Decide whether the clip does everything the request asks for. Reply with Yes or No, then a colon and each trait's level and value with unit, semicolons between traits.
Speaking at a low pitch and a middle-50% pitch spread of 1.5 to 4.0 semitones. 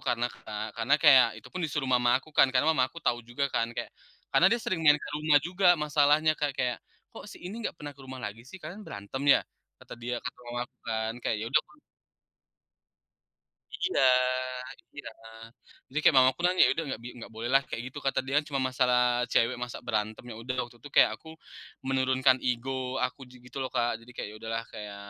Yes: low, 130 Hz; average, 3.7 semitones